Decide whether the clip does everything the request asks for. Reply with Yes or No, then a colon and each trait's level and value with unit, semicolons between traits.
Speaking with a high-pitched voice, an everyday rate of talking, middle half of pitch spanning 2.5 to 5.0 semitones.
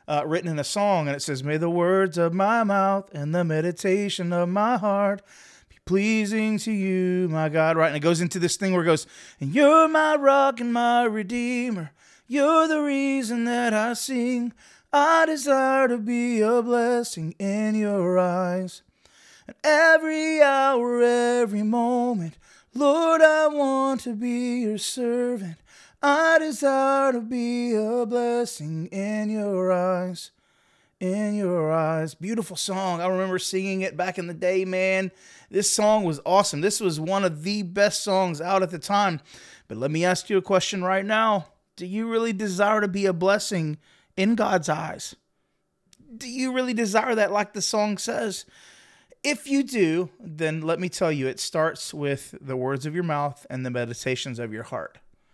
No: high, 200 Hz; average, 170 wpm; wide, 5.4 semitones